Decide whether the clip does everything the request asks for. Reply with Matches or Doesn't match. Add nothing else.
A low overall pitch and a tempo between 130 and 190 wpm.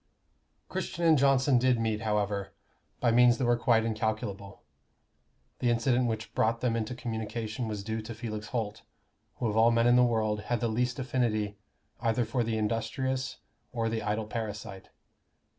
Matches